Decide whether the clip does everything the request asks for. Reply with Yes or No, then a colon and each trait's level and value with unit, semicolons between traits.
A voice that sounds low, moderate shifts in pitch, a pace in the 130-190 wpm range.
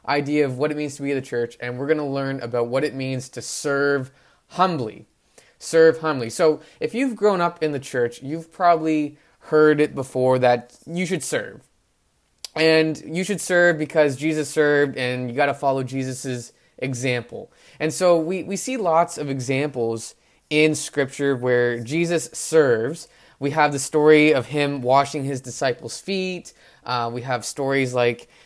No: medium, 145 Hz; average, 3.5 semitones; average, 175 wpm